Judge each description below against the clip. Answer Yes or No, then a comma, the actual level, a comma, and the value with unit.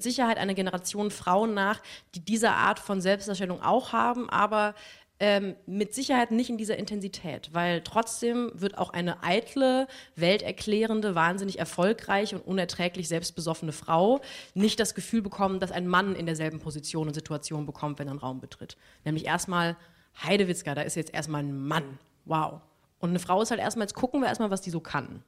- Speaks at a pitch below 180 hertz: No, high, 190 Hz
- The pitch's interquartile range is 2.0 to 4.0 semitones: No, average, 4.4 semitones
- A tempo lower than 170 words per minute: No, average, 180 wpm